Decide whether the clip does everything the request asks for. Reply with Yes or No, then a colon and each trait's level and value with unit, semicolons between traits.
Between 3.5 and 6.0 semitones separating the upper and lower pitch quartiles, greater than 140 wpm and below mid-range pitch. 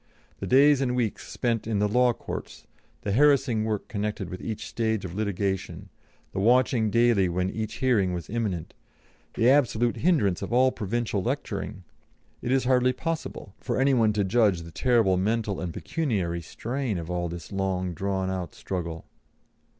Yes: average, 4.6 semitones; average, 165 wpm; low, 110 Hz